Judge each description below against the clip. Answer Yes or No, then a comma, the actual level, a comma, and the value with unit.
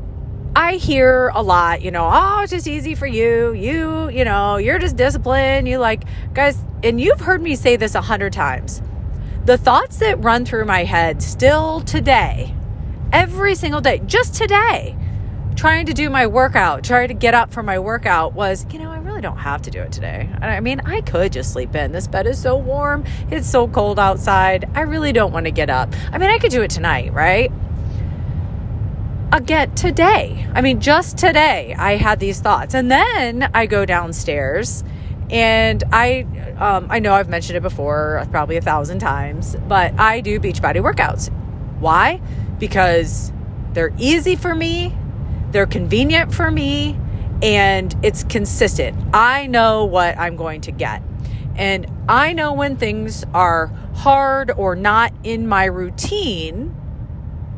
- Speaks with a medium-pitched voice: No, high, 195 Hz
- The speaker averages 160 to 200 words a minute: Yes, average, 170 wpm